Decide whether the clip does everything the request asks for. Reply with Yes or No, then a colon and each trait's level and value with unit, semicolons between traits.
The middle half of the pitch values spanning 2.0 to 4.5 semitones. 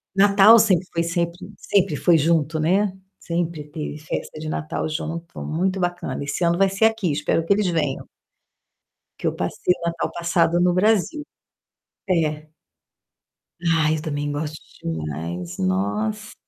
Yes: average, 3.4 semitones